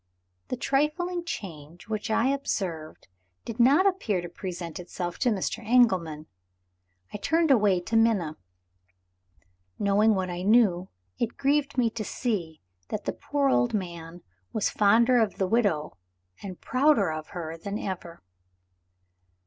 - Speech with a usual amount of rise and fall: No, wide, 5.7 semitones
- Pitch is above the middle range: Yes, high, 210 Hz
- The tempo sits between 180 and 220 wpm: No, average, 140 wpm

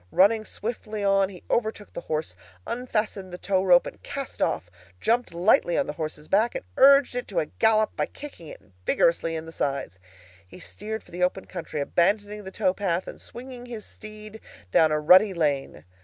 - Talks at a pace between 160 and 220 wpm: Yes, average, 185 wpm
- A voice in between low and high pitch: No, high, 195 Hz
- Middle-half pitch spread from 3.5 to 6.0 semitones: Yes, average, 4.7 semitones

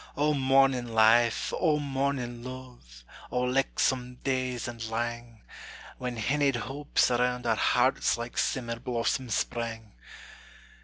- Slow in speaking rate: Yes, slow, 115 wpm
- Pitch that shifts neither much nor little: No, narrow, 2.2 semitones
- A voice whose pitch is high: No, low, 125 Hz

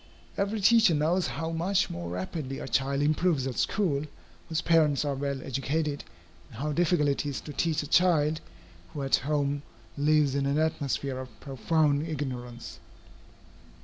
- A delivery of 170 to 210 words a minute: No, average, 155 wpm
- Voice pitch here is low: No, medium, 145 Hz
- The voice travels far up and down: No, average, 3.0 semitones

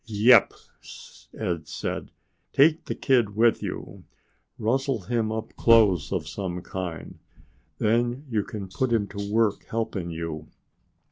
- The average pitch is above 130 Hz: No, low, 110 Hz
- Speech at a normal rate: No, slow, 130 wpm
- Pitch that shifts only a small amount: No, average, 4.0 semitones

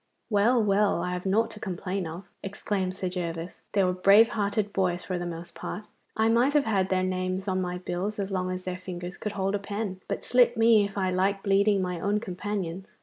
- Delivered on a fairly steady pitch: Yes, narrow, 2.1 semitones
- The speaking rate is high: Yes, fast, 220 wpm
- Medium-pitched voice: No, high, 195 Hz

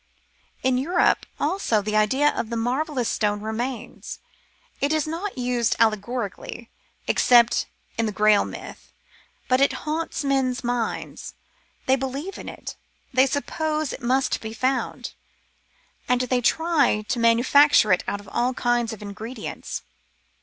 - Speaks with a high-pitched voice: Yes, very high, 250 Hz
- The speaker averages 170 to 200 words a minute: No, average, 140 wpm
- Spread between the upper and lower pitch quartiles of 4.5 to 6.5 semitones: No, average, 3.7 semitones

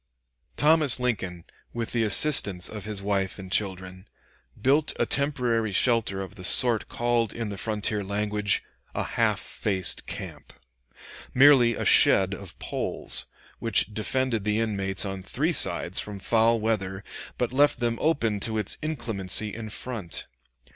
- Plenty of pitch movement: No, average, 3.5 semitones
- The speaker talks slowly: No, average, 145 wpm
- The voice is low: Yes, low, 110 Hz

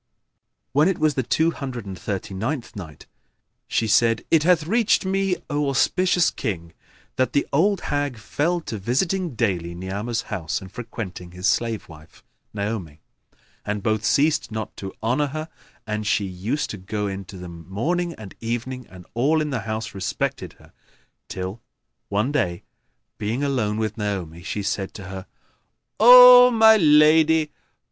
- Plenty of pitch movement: Yes, wide, 7.7 semitones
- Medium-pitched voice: No, low, 115 Hz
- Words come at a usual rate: Yes, average, 160 wpm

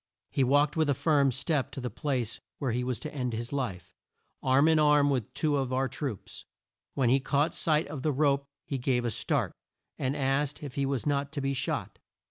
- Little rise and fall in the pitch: Yes, narrow, 2.2 semitones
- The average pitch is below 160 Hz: Yes, medium, 140 Hz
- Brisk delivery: Yes, fast, 215 wpm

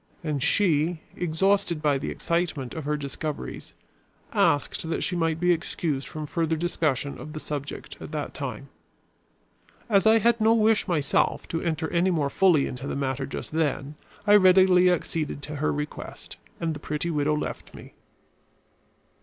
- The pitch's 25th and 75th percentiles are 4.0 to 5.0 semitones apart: No, average, 3.3 semitones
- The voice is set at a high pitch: No, medium, 160 Hz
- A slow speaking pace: No, average, 160 wpm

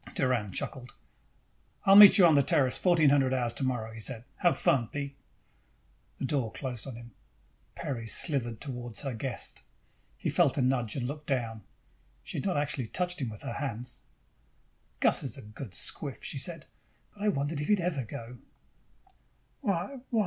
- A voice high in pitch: No, low, 135 Hz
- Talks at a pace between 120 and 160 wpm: No, average, 180 wpm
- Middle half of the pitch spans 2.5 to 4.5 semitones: Yes, average, 4.2 semitones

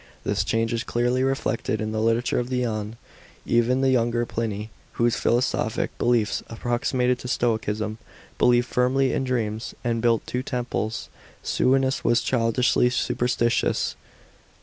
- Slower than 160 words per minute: Yes, slow, 135 wpm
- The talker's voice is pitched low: Yes, low, 120 Hz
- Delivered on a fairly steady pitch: Yes, narrow, 1.6 semitones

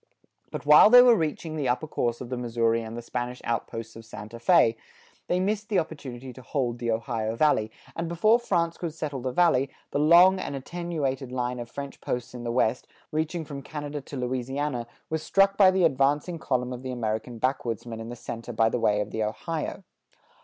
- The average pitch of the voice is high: No, low, 130 Hz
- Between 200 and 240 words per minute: Yes, fast, 205 wpm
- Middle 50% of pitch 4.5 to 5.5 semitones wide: Yes, average, 5.2 semitones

